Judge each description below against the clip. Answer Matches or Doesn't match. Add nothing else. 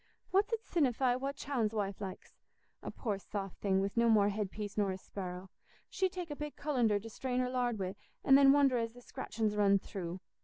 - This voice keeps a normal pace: Doesn't match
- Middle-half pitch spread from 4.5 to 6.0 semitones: Matches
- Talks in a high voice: Matches